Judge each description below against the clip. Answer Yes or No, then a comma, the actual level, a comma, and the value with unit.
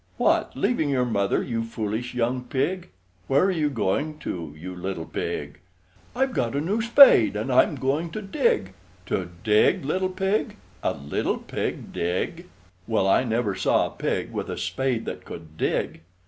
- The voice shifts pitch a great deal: Yes, wide, 8.8 semitones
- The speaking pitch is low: Yes, low, 125 Hz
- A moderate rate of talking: Yes, average, 170 wpm